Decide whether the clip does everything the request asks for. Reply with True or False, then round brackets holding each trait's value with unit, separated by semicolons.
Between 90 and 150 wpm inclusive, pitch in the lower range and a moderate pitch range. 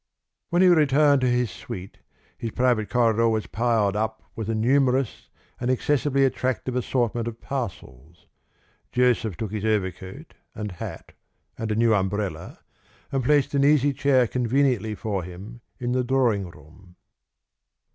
True (145 wpm; 120 Hz; 3.7 semitones)